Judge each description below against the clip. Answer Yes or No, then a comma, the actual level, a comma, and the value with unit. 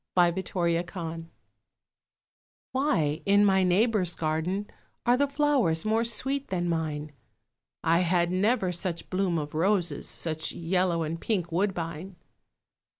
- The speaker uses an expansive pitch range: No, average, 3.6 semitones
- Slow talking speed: Yes, slow, 125 wpm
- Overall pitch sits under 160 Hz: No, medium, 180 Hz